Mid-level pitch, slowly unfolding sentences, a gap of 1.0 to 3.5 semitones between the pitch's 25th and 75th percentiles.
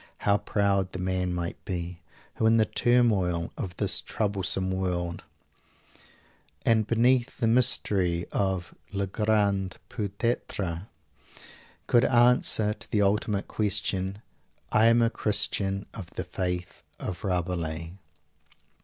No: low, 100 Hz; slow, 120 wpm; average, 3.2 semitones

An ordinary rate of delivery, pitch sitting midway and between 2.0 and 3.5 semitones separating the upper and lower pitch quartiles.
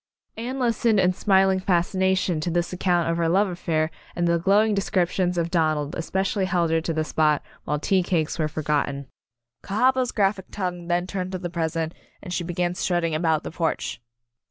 Yes: average, 185 wpm; medium, 175 Hz; average, 2.7 semitones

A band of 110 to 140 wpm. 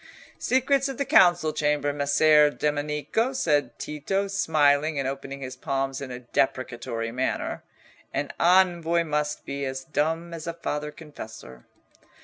Yes: slow, 135 wpm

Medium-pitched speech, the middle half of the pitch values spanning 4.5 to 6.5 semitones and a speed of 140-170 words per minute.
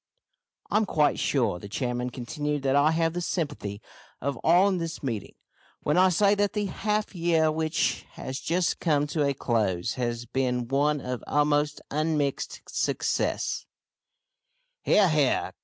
Yes: medium, 150 Hz; average, 5.1 semitones; average, 165 wpm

